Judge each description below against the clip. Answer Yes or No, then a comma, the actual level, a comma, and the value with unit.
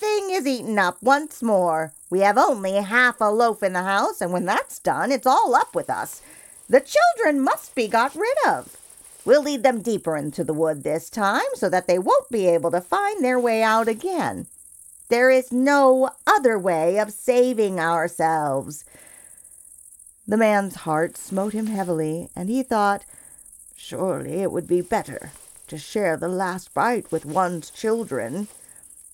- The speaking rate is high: No, average, 170 wpm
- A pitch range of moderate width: No, wide, 6.6 semitones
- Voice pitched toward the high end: Yes, high, 205 Hz